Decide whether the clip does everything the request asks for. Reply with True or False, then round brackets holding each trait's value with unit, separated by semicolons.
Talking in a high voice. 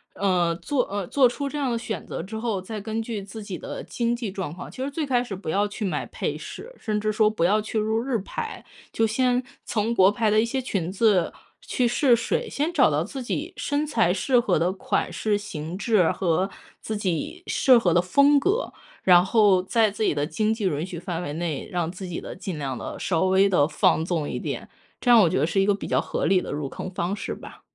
True (205 Hz)